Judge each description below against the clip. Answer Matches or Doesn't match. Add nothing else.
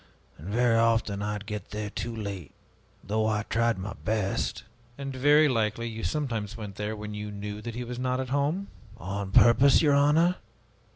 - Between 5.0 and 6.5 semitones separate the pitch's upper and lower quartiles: Doesn't match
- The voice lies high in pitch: Doesn't match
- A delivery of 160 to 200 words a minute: Matches